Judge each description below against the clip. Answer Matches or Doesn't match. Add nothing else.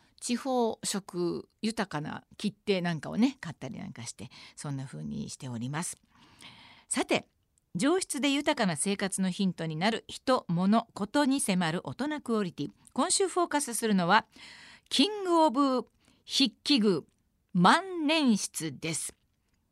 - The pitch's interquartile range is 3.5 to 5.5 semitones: Doesn't match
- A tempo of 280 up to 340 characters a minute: Doesn't match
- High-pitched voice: Matches